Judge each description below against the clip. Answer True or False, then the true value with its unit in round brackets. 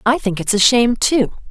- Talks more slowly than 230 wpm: False (240 wpm)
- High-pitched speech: True (230 Hz)